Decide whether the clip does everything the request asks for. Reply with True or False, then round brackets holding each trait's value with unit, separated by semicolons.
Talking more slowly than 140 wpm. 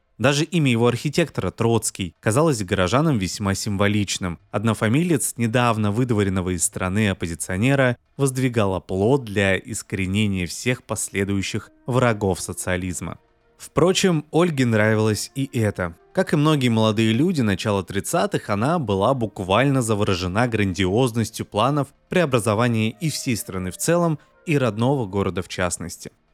True (120 wpm)